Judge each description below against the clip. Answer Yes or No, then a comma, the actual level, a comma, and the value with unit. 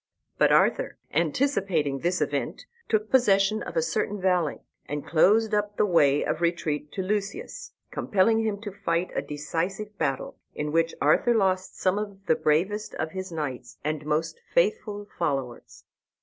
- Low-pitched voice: No, medium, 185 Hz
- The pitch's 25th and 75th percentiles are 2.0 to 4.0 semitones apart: No, average, 5.1 semitones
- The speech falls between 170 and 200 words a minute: No, average, 155 wpm